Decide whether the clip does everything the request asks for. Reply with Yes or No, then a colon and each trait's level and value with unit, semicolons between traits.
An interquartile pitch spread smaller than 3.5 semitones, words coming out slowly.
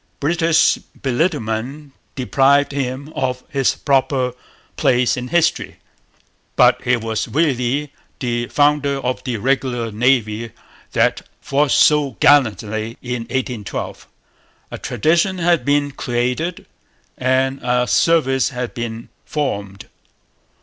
Yes: average, 3.1 semitones; slow, 110 wpm